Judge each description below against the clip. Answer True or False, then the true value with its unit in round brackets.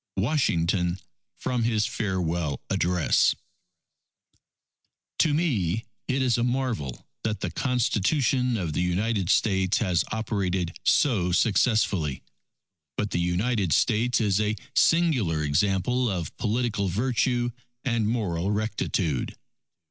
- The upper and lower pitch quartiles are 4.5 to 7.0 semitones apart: True (5.4 semitones)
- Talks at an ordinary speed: False (110 wpm)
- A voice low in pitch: True (105 Hz)